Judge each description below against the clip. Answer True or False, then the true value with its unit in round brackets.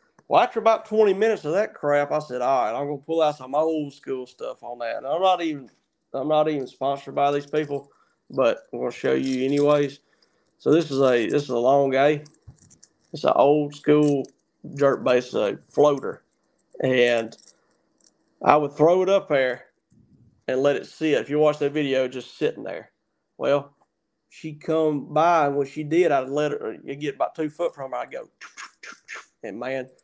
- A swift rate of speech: False (195 wpm)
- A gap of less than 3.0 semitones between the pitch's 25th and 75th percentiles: True (2.5 semitones)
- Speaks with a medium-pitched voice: True (145 Hz)